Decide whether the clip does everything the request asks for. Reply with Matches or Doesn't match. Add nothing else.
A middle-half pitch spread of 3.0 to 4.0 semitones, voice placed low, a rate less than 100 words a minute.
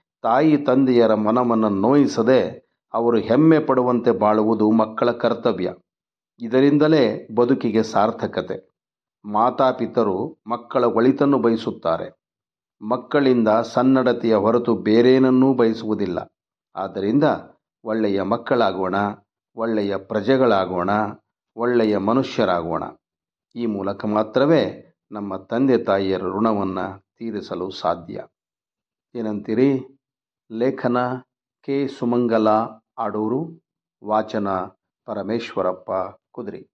Matches